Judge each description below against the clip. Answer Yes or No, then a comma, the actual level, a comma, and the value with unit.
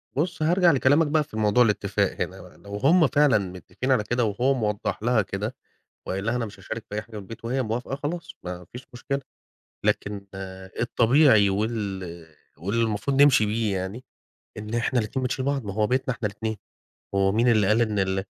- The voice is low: Yes, low, 115 Hz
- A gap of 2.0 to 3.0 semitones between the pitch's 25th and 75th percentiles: No, average, 4.2 semitones